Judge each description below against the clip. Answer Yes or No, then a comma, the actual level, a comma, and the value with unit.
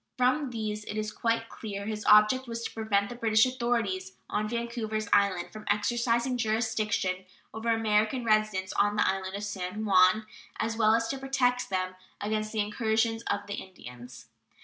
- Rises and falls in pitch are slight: Yes, narrow, 2.2 semitones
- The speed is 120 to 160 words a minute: No, average, 170 wpm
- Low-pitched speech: No, high, 215 Hz